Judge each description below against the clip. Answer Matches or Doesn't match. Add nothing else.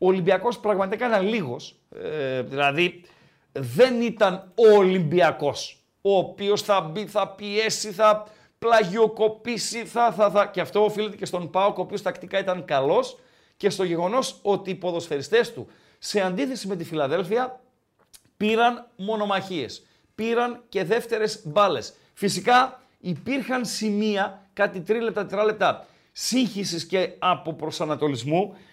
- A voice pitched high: Matches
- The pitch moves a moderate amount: Matches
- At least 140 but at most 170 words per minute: Doesn't match